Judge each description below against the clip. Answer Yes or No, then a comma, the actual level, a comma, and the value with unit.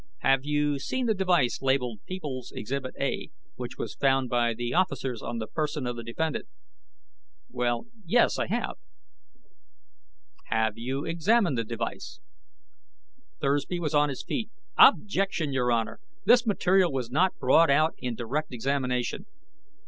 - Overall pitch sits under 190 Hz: Yes, medium, 140 Hz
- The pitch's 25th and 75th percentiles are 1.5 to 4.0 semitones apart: No, average, 5.2 semitones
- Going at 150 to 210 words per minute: No, average, 140 wpm